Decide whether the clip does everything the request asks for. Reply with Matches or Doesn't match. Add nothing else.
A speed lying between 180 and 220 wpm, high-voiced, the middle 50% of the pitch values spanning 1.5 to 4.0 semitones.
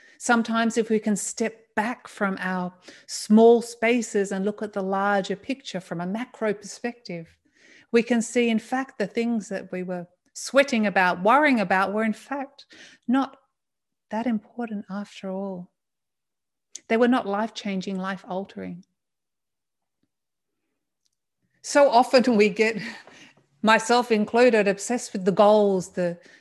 Doesn't match